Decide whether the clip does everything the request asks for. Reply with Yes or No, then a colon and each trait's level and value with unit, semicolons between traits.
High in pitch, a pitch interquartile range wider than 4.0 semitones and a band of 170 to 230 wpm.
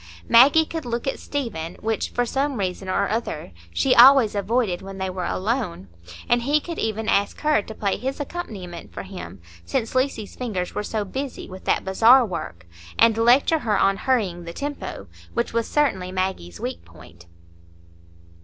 Yes: high, 220 Hz; wide, 5.6 semitones; average, 175 wpm